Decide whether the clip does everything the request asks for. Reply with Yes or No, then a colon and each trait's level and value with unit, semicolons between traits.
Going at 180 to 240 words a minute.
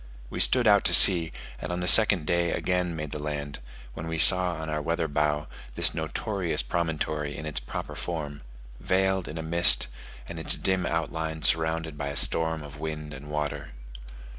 Yes: average, 185 wpm